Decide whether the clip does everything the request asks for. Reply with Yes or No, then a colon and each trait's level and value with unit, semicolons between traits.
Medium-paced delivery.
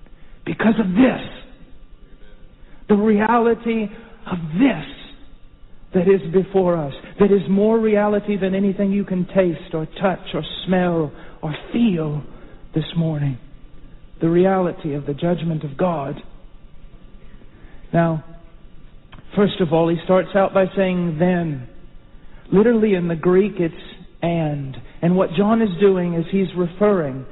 No: slow, 130 wpm